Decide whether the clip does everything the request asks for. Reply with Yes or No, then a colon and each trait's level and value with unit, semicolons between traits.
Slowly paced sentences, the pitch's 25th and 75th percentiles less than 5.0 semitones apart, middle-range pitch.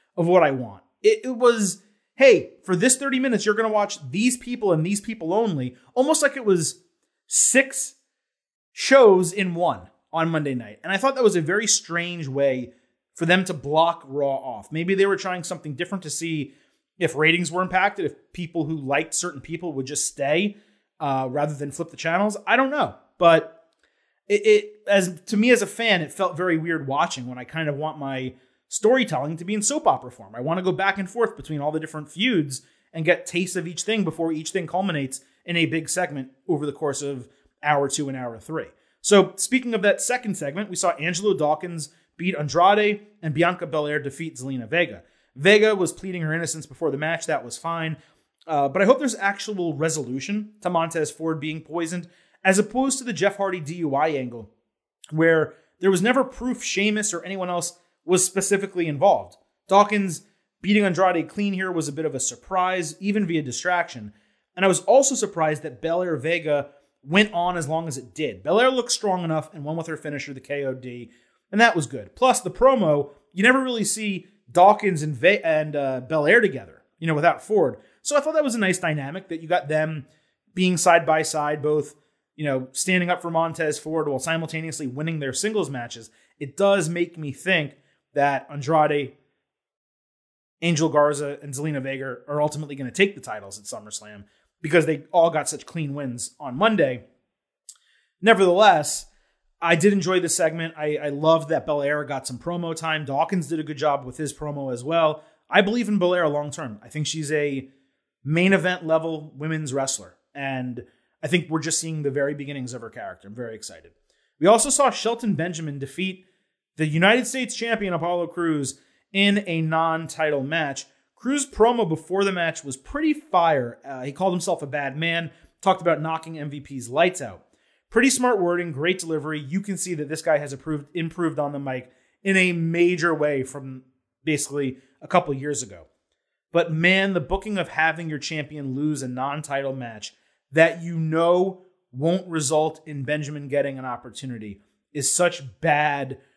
No: average, 190 wpm; average, 4.6 semitones; medium, 165 Hz